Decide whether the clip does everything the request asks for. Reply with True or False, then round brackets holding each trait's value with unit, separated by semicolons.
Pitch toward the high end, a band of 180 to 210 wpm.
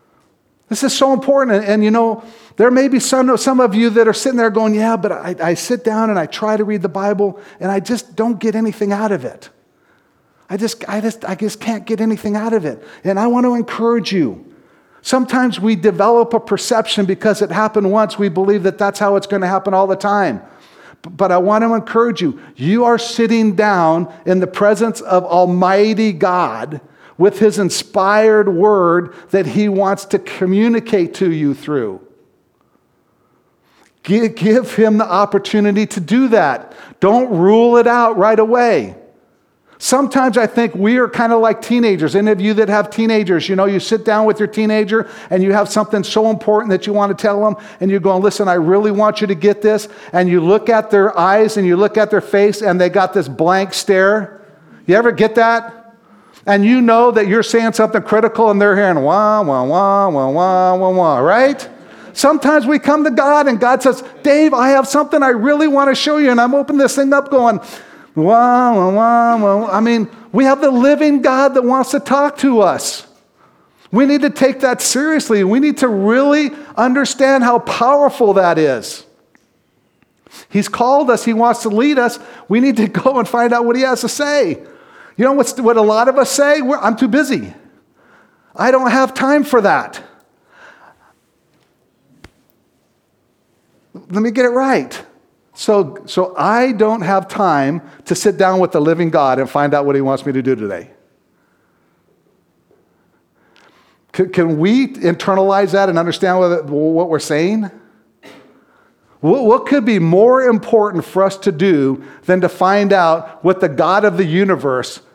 True (215 Hz; 190 wpm)